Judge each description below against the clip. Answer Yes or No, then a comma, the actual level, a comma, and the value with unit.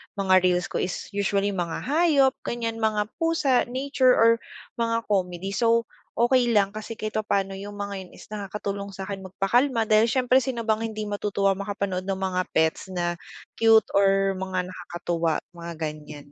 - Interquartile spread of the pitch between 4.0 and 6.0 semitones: No, average, 3.4 semitones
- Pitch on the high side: Yes, high, 200 Hz